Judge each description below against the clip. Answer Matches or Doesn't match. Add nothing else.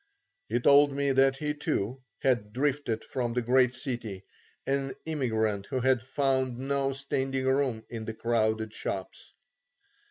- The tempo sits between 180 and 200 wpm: Doesn't match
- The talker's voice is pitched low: Matches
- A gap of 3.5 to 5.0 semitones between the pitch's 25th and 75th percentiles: Doesn't match